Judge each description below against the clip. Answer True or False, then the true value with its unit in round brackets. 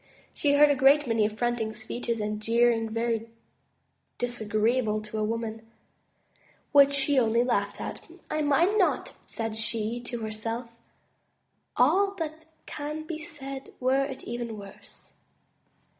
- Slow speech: True (130 wpm)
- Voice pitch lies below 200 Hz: False (240 Hz)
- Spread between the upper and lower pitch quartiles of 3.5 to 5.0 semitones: True (4.3 semitones)